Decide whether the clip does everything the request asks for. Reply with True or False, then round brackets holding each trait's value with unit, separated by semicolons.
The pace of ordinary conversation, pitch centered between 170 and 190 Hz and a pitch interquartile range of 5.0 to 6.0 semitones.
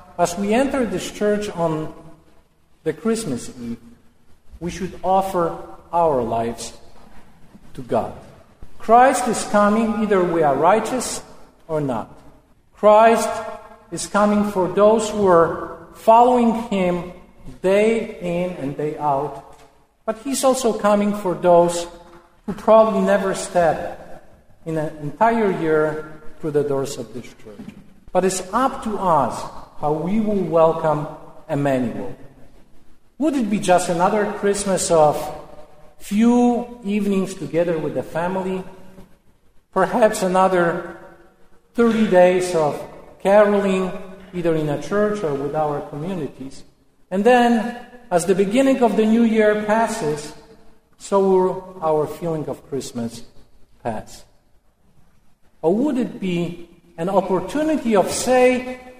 True (125 wpm; 185 Hz; 5.5 semitones)